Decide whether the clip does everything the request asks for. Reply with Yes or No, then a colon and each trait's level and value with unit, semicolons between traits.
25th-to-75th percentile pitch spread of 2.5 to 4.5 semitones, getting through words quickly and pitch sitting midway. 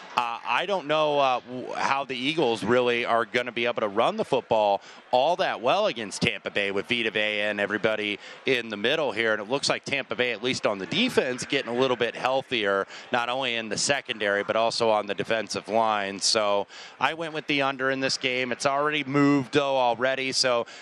No: average, 4.1 semitones; fast, 215 wpm; low, 120 Hz